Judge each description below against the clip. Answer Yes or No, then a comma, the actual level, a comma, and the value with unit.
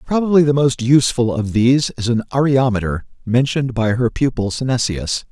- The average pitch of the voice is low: Yes, low, 125 Hz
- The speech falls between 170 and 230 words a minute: No, average, 160 wpm